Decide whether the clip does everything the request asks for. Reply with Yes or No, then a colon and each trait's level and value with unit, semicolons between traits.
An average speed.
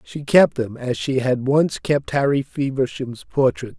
Yes: average, 175 wpm